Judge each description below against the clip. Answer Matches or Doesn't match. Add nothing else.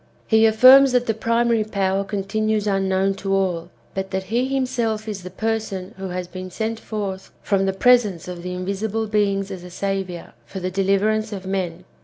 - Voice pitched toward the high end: Matches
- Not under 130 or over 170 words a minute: Doesn't match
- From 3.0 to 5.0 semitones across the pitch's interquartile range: Doesn't match